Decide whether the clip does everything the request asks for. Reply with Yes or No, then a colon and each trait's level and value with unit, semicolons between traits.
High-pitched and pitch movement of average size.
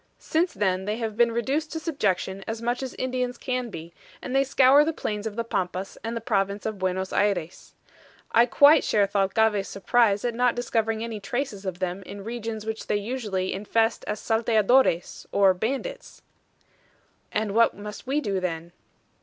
Yes: high, 220 Hz; average, 3.7 semitones